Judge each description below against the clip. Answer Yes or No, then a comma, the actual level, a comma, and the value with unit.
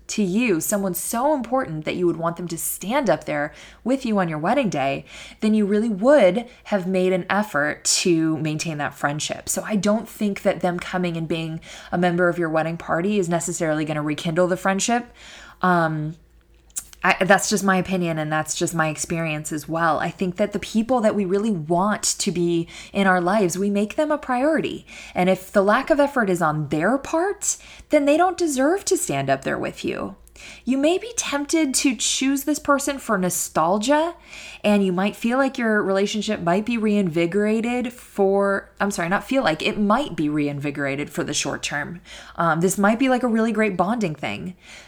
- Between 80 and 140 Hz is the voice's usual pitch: No, high, 195 Hz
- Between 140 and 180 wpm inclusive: No, average, 200 wpm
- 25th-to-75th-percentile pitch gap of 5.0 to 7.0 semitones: Yes, wide, 5.6 semitones